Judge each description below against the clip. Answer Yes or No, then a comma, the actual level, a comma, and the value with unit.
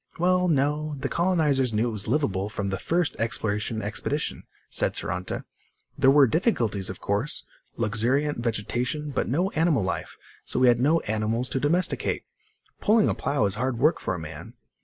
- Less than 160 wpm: No, average, 170 wpm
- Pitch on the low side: Yes, low, 130 Hz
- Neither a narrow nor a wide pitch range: No, wide, 6.0 semitones